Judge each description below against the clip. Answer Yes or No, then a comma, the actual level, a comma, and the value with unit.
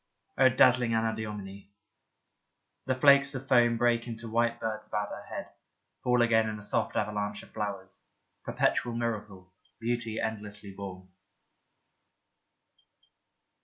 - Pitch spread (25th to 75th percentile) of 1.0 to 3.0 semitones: Yes, narrow, 2.5 semitones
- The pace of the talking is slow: Yes, slow, 120 wpm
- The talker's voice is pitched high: No, low, 110 Hz